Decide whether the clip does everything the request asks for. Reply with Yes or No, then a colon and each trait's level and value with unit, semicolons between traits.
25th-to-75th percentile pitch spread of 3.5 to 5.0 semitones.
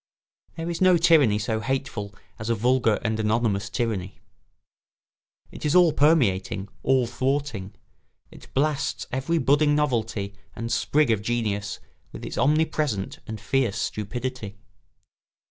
No: wide, 5.6 semitones